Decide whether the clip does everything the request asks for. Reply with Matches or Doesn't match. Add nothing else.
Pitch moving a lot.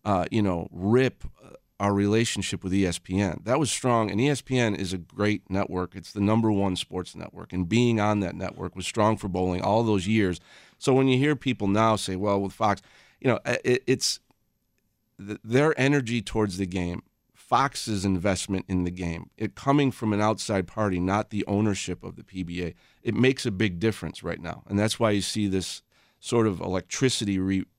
Doesn't match